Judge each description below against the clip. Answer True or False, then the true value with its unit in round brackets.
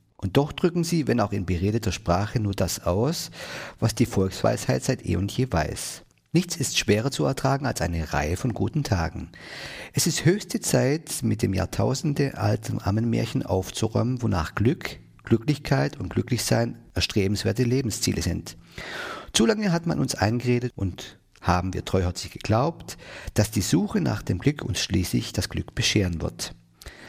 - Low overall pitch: True (110 Hz)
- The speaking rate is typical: True (160 wpm)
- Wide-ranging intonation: True (6.0 semitones)